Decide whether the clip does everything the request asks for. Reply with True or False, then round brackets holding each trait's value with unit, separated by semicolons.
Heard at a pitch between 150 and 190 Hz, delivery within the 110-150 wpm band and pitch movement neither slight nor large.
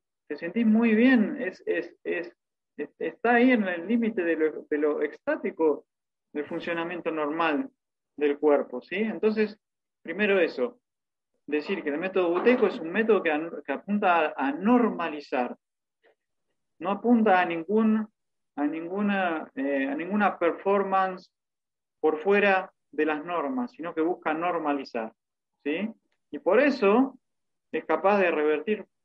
False (185 Hz; 140 wpm; 5.8 semitones)